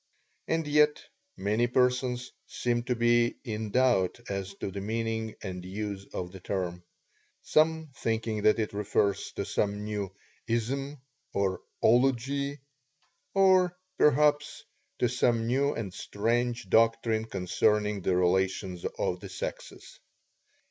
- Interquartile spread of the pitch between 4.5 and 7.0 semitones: No, average, 4.1 semitones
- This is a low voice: Yes, low, 115 Hz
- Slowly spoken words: Yes, slow, 125 wpm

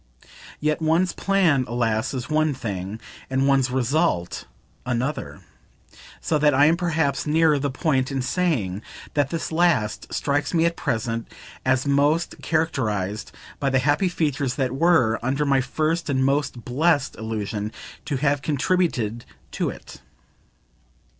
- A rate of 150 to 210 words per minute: No, average, 140 wpm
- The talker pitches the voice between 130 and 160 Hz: Yes, medium, 140 Hz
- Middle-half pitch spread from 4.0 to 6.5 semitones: Yes, average, 4.4 semitones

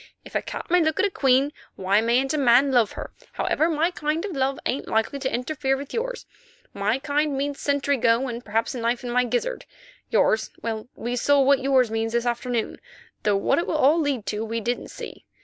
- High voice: Yes, very high, 265 Hz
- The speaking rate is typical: No, fast, 215 wpm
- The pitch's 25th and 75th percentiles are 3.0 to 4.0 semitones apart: Yes, average, 3.7 semitones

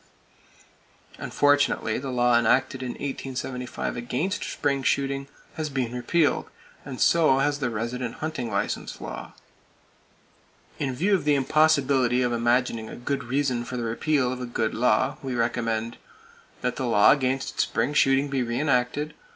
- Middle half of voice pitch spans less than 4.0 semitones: Yes, average, 2.8 semitones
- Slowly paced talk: No, average, 150 wpm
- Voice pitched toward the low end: Yes, low, 130 Hz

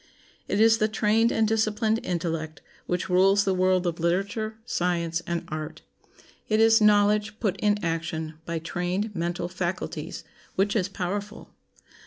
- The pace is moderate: Yes, average, 145 wpm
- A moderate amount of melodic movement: Yes, average, 3.6 semitones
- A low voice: No, high, 190 Hz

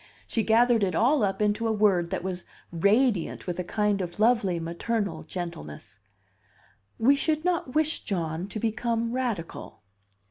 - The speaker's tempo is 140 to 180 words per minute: Yes, average, 150 wpm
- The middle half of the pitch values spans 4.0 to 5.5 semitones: Yes, average, 5.0 semitones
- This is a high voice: Yes, high, 210 Hz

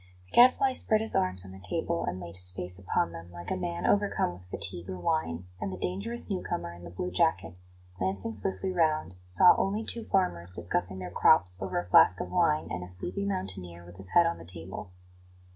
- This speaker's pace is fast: Yes, fast, 215 wpm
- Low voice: Yes, very low, 90 Hz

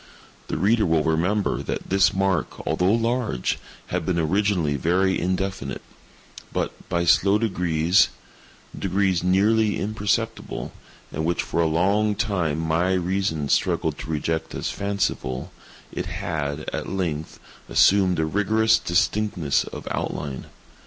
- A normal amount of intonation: Yes, average, 3.9 semitones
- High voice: No, very low, 90 Hz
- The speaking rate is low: Yes, slow, 120 wpm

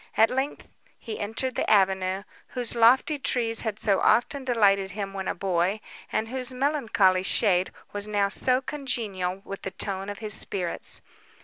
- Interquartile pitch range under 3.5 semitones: No, average, 4.0 semitones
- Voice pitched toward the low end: No, high, 210 Hz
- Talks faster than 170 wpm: No, average, 165 wpm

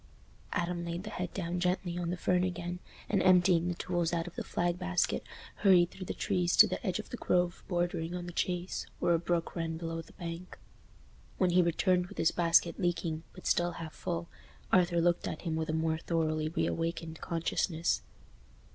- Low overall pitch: No, medium, 175 Hz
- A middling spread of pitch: No, narrow, 1.2 semitones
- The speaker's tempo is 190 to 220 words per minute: Yes, average, 195 wpm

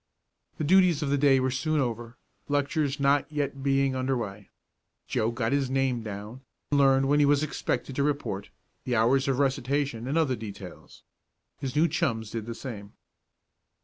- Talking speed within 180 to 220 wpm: No, average, 170 wpm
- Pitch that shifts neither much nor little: Yes, average, 3.4 semitones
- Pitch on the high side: No, low, 135 Hz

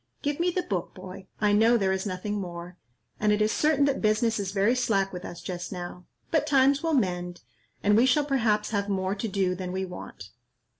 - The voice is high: Yes, high, 205 Hz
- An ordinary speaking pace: No, fast, 215 wpm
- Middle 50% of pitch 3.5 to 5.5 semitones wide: Yes, average, 4.8 semitones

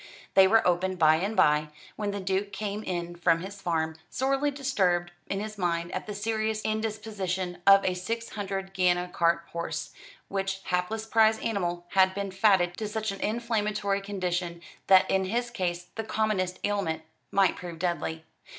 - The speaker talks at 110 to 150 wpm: No, average, 170 wpm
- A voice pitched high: Yes, high, 195 Hz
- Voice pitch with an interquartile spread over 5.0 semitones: No, average, 3.3 semitones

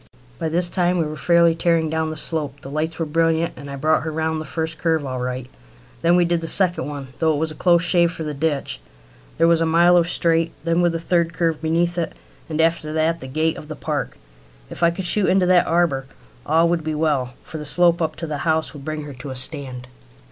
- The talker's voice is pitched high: No, medium, 160 Hz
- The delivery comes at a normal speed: No, fast, 250 wpm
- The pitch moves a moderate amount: No, narrow, 1.9 semitones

